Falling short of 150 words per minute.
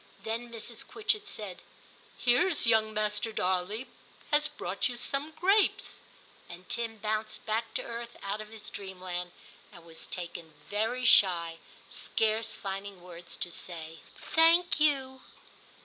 Yes: average, 140 wpm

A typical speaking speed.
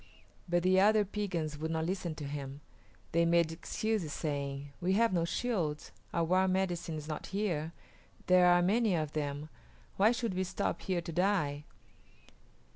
Yes: average, 165 wpm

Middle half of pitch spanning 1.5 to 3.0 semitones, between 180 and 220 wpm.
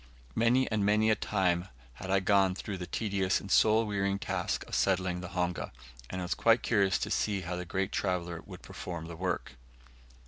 Yes: narrow, 2.4 semitones; average, 200 wpm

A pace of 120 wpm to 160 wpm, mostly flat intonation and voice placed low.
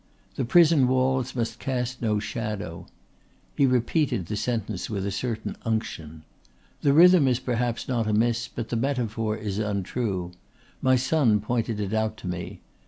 No: average, 155 wpm; average, 3.2 semitones; low, 115 Hz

